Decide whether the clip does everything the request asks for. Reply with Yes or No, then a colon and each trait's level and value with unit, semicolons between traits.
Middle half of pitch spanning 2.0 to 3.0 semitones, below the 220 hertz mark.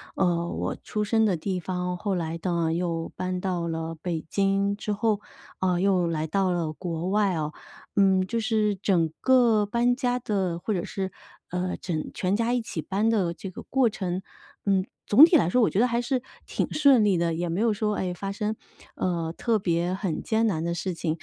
No: average, 3.7 semitones; high, 190 Hz